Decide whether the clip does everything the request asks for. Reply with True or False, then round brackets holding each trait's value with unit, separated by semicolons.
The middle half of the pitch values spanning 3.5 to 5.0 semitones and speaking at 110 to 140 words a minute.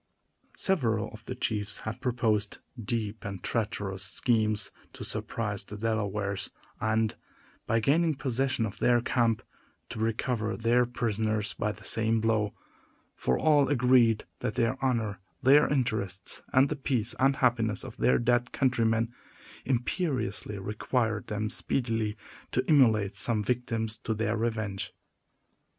False (2.7 semitones; 135 wpm)